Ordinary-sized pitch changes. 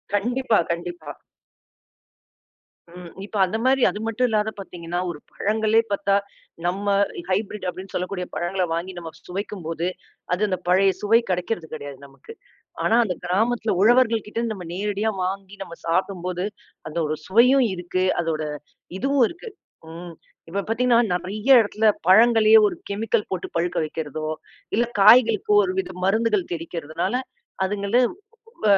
Yes: average, 4.0 semitones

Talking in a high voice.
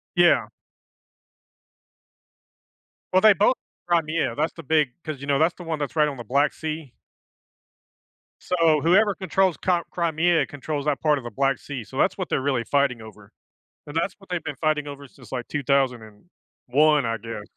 No: medium, 150 Hz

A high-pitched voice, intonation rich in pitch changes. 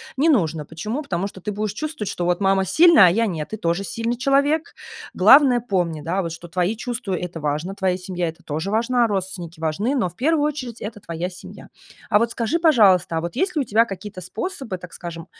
Yes: high, 195 Hz; wide, 5.7 semitones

